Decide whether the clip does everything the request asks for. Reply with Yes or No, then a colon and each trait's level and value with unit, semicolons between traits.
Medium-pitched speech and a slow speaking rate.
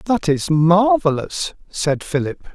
Yes: medium, 170 Hz; slow, 120 wpm